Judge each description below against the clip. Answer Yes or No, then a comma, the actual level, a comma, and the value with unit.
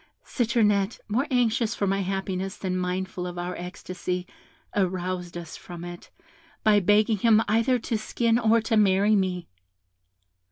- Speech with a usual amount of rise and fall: Yes, average, 3.4 semitones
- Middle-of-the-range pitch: No, high, 195 Hz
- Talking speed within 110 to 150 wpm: Yes, average, 145 wpm